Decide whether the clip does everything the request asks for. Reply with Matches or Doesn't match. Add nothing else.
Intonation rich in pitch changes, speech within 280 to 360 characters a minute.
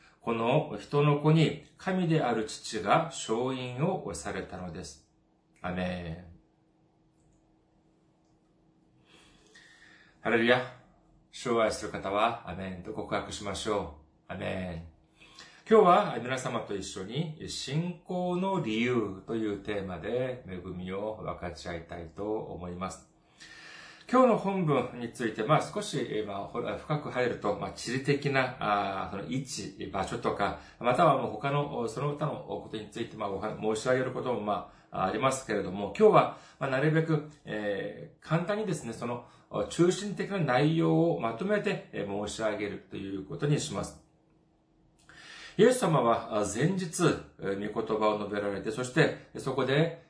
Doesn't match